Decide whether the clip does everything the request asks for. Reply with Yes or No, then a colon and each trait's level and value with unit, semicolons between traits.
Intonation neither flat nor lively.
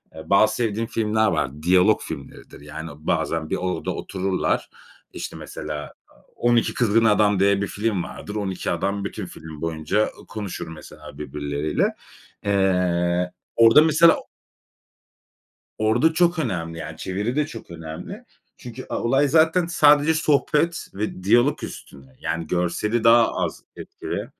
No: wide, 6.0 semitones